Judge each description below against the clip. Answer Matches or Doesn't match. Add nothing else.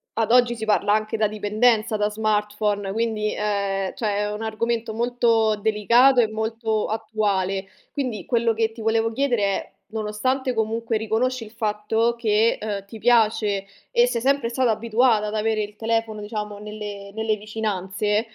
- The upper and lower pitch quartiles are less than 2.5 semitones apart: Matches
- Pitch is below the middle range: Doesn't match